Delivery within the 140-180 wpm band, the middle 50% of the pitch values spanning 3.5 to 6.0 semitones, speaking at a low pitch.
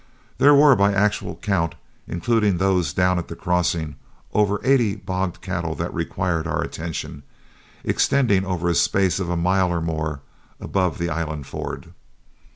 No: average, 155 wpm; average, 2.9 semitones; very low, 90 Hz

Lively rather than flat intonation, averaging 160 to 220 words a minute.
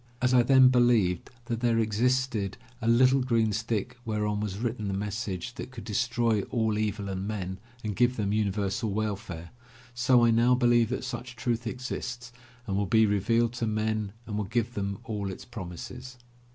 No: average, 2.8 semitones; average, 180 wpm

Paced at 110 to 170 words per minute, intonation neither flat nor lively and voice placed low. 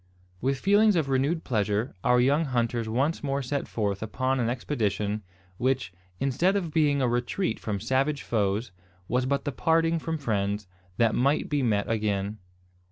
Yes: average, 165 wpm; average, 4.8 semitones; low, 125 Hz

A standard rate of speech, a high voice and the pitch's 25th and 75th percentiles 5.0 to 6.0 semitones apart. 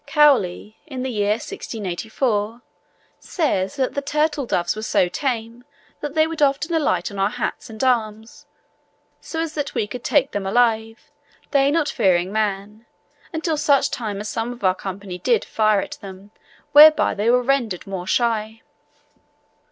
Yes: average, 160 wpm; high, 225 Hz; average, 5.3 semitones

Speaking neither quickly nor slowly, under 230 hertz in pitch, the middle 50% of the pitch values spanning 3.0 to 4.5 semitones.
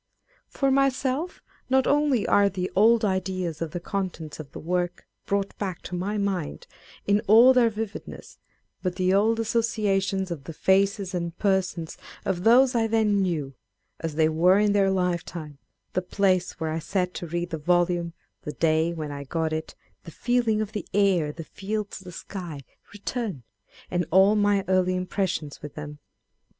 Yes: average, 175 wpm; medium, 185 Hz; average, 3.6 semitones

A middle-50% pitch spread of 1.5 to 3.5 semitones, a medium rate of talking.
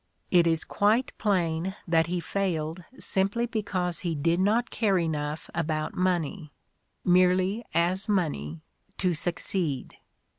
No: average, 3.1 semitones; slow, 125 wpm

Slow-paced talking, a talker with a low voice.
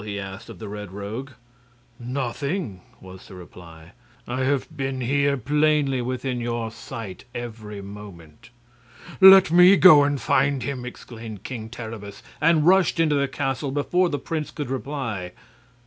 No: average, 150 wpm; low, 125 Hz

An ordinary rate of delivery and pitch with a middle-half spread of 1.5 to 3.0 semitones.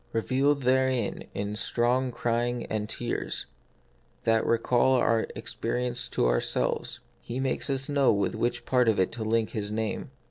Yes: average, 155 wpm; narrow, 2.5 semitones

